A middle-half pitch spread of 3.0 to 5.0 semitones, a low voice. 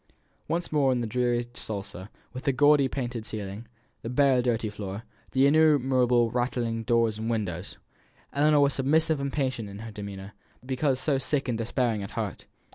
Yes: average, 3.7 semitones; low, 125 Hz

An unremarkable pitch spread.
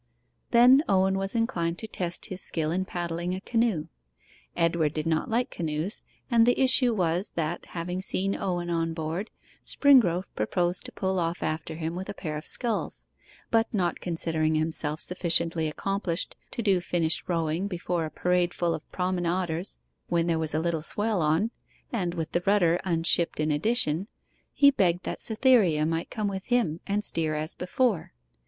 Yes: average, 3.3 semitones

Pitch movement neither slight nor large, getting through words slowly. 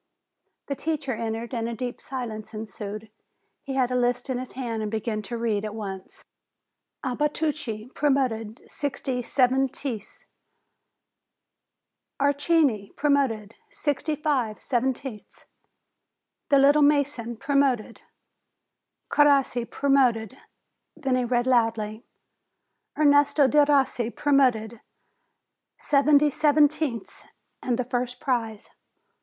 Yes: average, 3.9 semitones; slow, 100 wpm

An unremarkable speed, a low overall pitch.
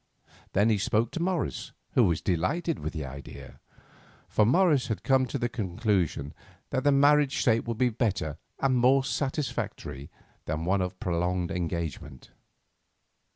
Yes: average, 150 wpm; low, 110 Hz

